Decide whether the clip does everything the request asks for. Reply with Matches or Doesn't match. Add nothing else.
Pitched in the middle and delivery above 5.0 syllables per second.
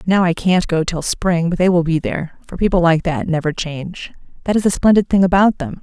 Matches